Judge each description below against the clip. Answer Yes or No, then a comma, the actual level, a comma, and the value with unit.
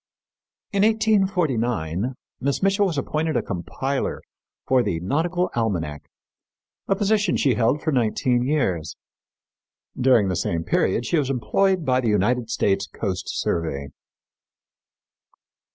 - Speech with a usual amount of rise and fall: No, wide, 8.7 semitones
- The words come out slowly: Yes, slow, 120 wpm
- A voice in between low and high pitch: No, low, 125 Hz